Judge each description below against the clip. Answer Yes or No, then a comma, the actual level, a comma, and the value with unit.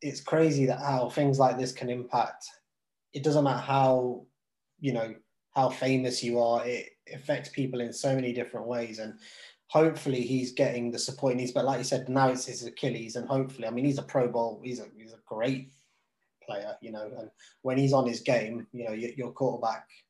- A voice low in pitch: Yes, low, 125 Hz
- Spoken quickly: Yes, fast, 210 wpm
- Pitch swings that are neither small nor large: No, narrow, 2.2 semitones